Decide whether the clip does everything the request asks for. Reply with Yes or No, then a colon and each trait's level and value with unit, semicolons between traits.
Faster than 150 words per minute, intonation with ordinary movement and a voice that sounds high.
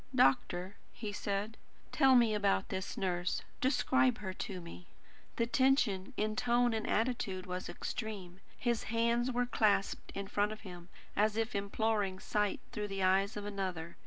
Yes: average, 160 wpm; average, 3.5 semitones; high, 205 Hz